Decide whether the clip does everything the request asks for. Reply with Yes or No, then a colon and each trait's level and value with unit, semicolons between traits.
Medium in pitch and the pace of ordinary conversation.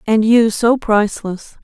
No: high, 215 Hz; average, 145 wpm